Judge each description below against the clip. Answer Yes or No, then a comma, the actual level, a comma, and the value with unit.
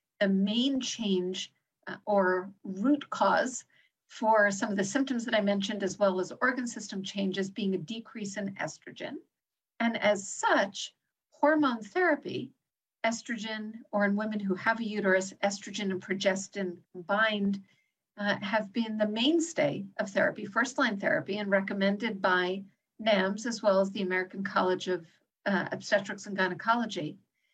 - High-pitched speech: Yes, high, 205 Hz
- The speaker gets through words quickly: No, average, 150 wpm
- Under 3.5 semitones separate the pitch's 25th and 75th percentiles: Yes, average, 2.8 semitones